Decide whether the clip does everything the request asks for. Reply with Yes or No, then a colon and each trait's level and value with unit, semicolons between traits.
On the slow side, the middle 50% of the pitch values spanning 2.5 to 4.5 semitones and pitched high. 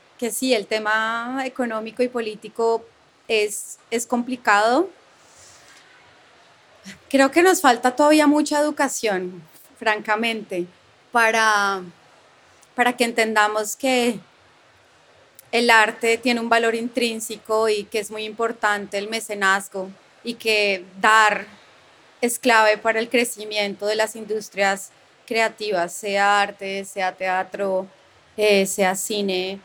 Yes: slow, 110 wpm; average, 2.8 semitones; high, 220 Hz